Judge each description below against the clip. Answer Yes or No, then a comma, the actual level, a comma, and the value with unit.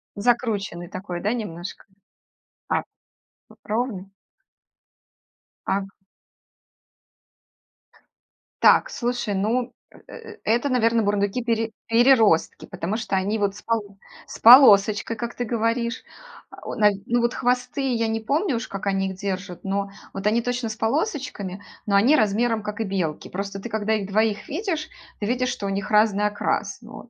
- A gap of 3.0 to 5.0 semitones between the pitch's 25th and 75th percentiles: Yes, average, 3.4 semitones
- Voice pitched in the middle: No, high, 220 Hz